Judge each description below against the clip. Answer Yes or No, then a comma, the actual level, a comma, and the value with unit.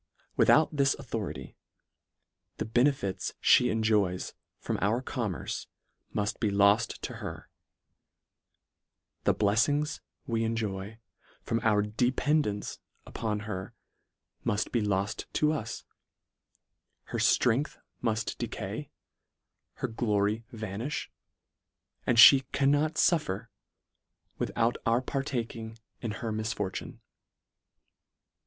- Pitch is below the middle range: Yes, low, 115 Hz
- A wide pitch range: No, average, 3.2 semitones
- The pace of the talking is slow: Yes, slow, 100 wpm